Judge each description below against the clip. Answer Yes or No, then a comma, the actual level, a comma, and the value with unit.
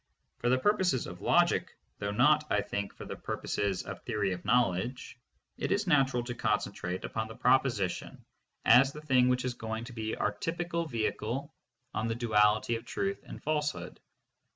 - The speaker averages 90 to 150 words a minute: No, average, 175 wpm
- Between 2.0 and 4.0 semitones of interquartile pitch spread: No, average, 4.4 semitones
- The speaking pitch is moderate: No, low, 120 Hz